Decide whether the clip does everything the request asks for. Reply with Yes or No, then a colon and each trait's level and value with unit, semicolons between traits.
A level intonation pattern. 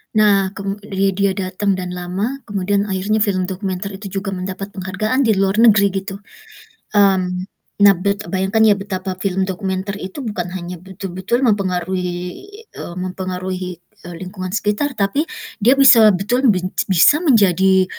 Yes: narrow, 2.0 semitones